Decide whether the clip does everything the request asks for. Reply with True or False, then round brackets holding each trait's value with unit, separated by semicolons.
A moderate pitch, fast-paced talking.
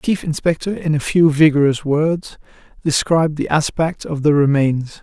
False (155 Hz; 165 wpm)